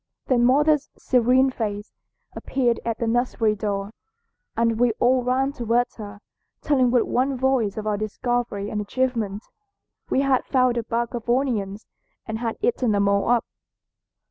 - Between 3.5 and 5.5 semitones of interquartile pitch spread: No, average, 3.0 semitones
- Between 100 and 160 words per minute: Yes, average, 155 wpm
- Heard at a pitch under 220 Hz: No, high, 240 Hz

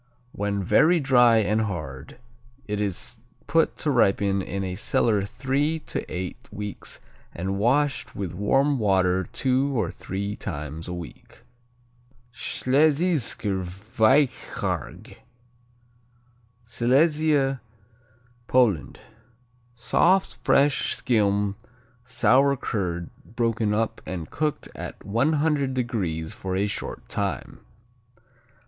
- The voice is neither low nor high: No, low, 110 Hz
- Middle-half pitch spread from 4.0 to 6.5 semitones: Yes, wide, 5.6 semitones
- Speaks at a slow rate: Yes, slow, 100 wpm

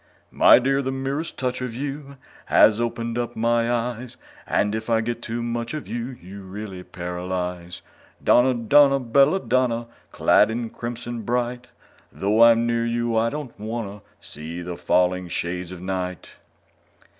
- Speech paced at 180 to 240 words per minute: No, average, 155 wpm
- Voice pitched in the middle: No, low, 115 Hz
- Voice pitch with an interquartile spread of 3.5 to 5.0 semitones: Yes, average, 3.9 semitones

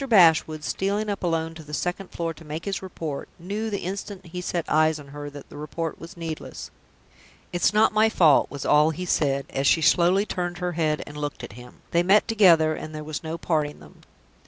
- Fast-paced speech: Yes, fast, 215 wpm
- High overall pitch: No, medium, 165 Hz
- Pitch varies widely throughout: No, average, 3.4 semitones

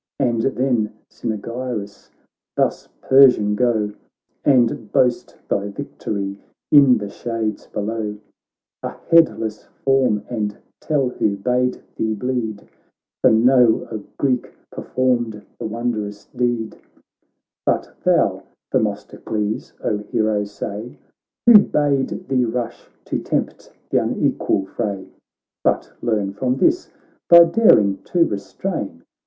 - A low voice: Yes, low, 115 Hz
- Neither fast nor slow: No, slow, 115 wpm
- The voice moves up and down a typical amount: Yes, average, 3.6 semitones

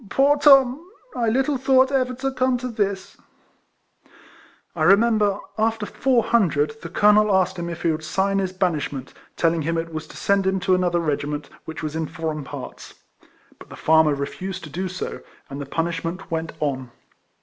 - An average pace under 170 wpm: No, average, 190 wpm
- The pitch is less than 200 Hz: Yes, medium, 185 Hz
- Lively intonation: Yes, wide, 6.0 semitones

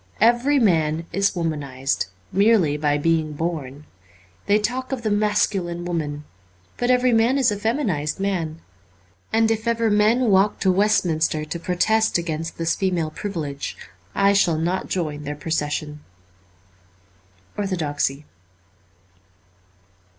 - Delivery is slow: Yes, slow, 130 wpm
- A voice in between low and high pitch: Yes, medium, 175 Hz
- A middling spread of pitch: No, wide, 5.7 semitones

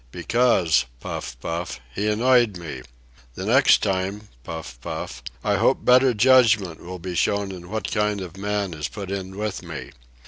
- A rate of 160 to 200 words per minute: No, average, 145 wpm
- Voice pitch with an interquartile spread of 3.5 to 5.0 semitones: Yes, average, 4.3 semitones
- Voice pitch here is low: Yes, very low, 95 Hz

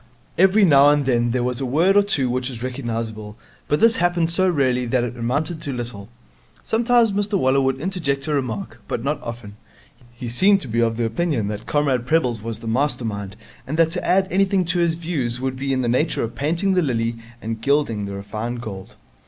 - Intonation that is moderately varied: No, wide, 6.0 semitones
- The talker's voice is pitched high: No, low, 130 Hz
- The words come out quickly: Yes, fast, 215 wpm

